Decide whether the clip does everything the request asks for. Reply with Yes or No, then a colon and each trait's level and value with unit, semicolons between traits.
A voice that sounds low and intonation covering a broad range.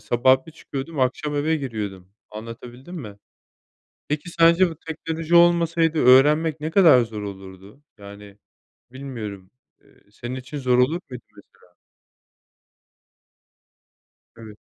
Yes: low, 130 Hz; wide, 6.8 semitones